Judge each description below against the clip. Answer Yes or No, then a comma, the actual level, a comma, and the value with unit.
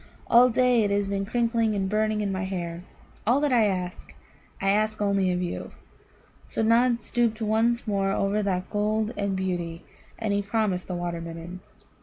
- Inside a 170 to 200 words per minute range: Yes, average, 180 wpm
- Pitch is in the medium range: No, high, 205 Hz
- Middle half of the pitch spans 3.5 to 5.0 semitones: No, average, 2.9 semitones